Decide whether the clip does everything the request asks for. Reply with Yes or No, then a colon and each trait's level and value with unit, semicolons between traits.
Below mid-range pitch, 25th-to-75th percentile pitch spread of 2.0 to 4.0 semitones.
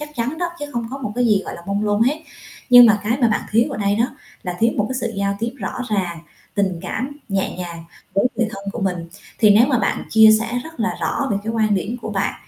No: high, 215 Hz; average, 3.2 semitones